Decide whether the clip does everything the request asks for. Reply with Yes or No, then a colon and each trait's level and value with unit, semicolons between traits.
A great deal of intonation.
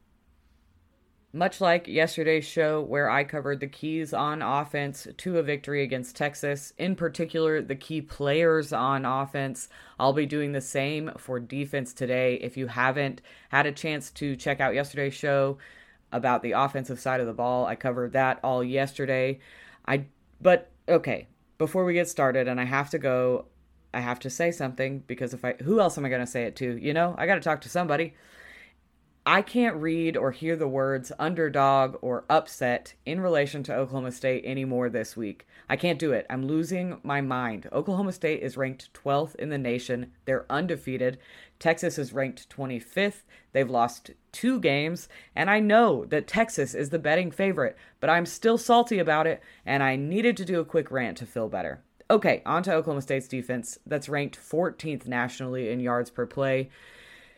No: average, 3.7 semitones